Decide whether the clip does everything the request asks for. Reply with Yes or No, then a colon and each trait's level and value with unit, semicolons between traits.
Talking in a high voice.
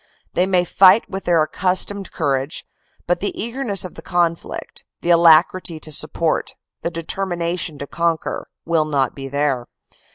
No: medium, 170 Hz